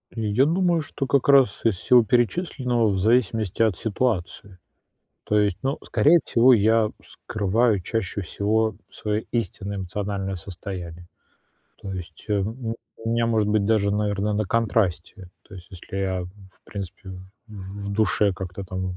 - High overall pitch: No, low, 105 Hz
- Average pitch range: Yes, average, 3.1 semitones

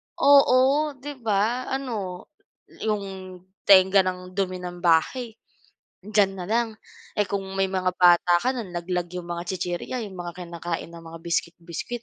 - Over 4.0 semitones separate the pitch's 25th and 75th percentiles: No, average, 3.4 semitones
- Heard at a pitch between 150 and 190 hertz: Yes, medium, 185 Hz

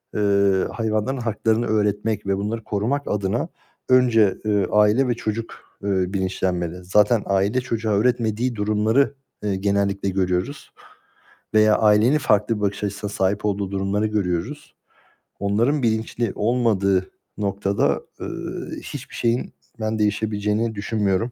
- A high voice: No, low, 105 Hz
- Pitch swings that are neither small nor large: No, narrow, 2.2 semitones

